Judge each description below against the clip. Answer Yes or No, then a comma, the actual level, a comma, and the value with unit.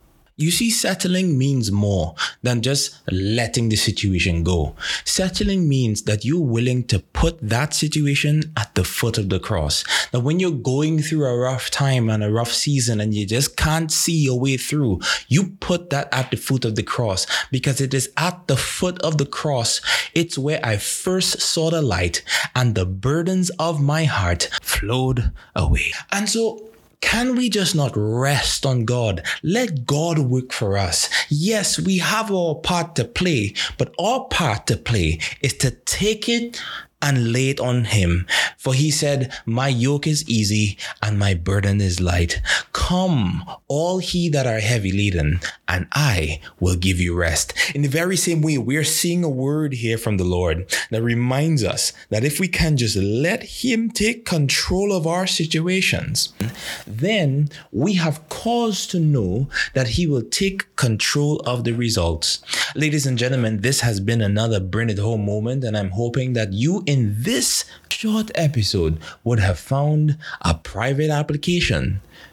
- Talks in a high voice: No, low, 135 Hz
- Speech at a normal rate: Yes, average, 175 wpm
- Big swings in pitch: Yes, wide, 6.7 semitones